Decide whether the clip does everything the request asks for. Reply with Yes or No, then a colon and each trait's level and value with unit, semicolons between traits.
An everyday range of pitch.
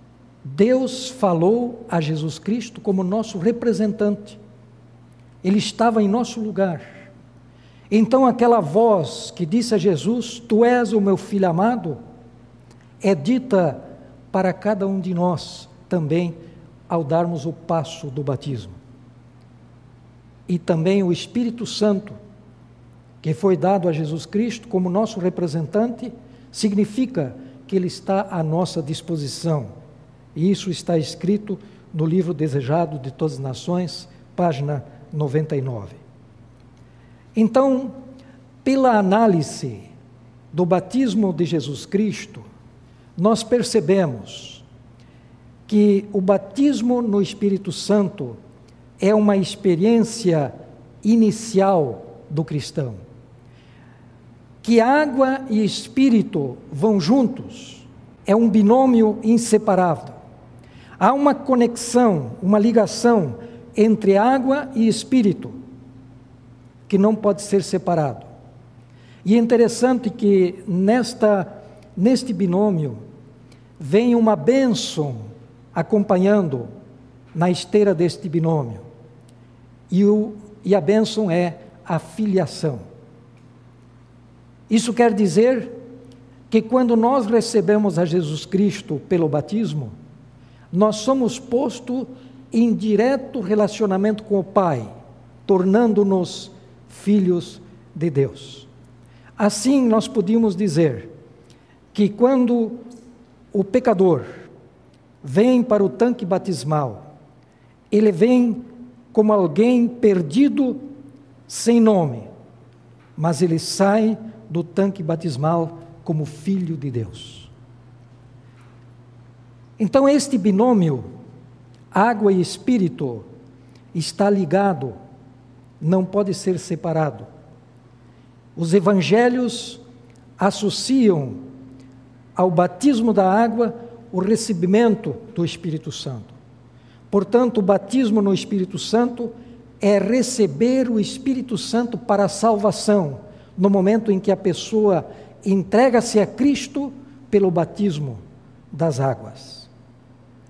No: wide, 8.9 semitones